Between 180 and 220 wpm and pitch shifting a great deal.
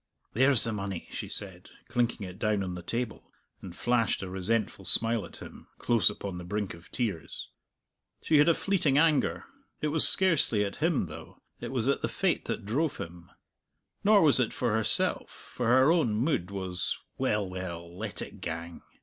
Yes: average, 185 wpm; wide, 6.0 semitones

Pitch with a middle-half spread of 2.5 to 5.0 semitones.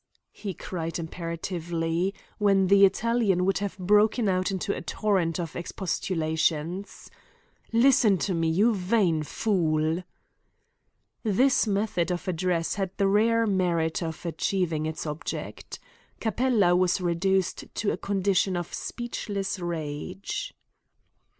Yes: average, 3.2 semitones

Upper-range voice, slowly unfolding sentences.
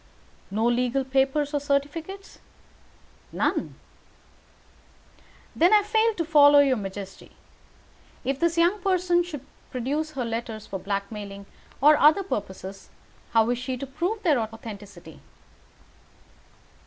Yes: very high, 275 Hz; slow, 115 wpm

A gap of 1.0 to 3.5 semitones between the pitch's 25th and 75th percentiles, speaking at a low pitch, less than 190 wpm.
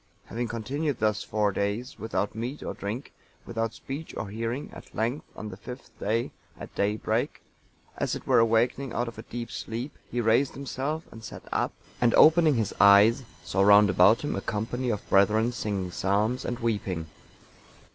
Yes: average, 3.0 semitones; low, 115 Hz; average, 175 wpm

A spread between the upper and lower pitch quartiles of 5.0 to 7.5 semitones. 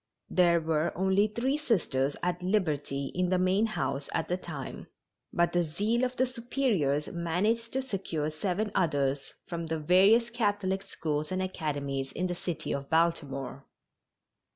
Yes: average, 5.3 semitones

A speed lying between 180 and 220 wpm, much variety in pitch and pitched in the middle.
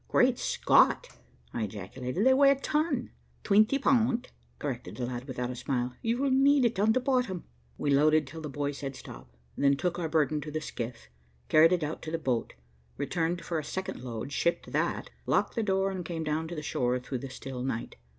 Yes: average, 200 wpm; wide, 7.6 semitones; medium, 155 Hz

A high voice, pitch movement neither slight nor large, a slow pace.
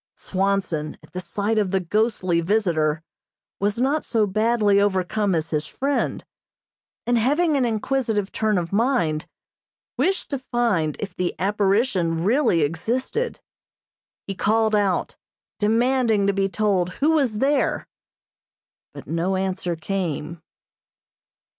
Yes: high, 205 Hz; average, 4.7 semitones; slow, 120 wpm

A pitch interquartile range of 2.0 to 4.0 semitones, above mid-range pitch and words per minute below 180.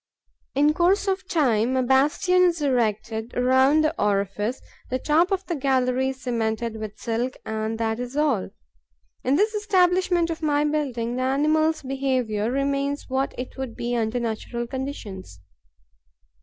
No: average, 4.7 semitones; very high, 260 Hz; average, 150 wpm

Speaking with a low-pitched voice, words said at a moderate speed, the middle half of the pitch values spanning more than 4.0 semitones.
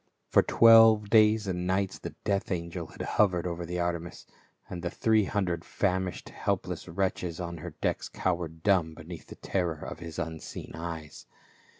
No: very low, 90 Hz; average, 175 wpm; average, 2.7 semitones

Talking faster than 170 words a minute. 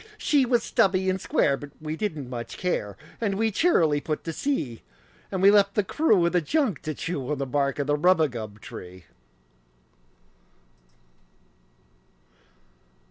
No: average, 145 wpm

